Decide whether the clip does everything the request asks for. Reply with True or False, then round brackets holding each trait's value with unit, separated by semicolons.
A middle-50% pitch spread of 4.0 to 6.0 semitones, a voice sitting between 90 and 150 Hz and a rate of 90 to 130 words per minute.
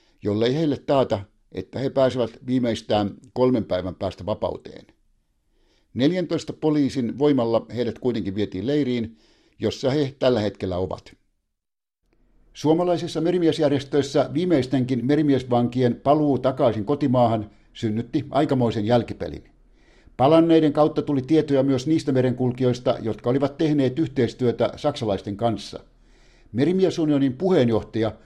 True (4.8 semitones; 125 Hz; 100 wpm)